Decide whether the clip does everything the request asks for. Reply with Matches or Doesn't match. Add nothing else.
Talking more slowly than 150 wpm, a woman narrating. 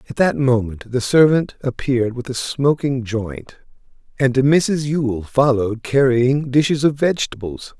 Doesn't match